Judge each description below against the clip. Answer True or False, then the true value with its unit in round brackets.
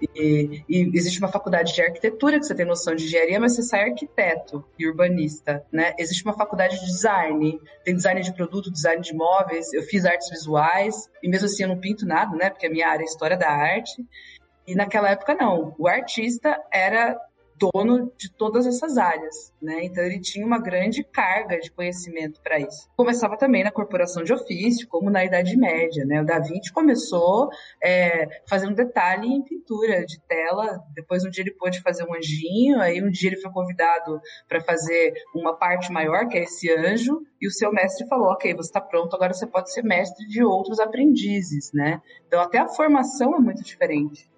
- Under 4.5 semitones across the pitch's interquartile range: False (5.2 semitones)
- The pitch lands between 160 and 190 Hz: True (185 Hz)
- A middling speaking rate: False (195 wpm)